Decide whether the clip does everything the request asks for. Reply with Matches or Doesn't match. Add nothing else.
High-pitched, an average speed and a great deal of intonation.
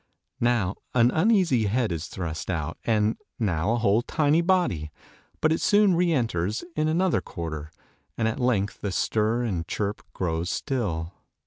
Doesn't match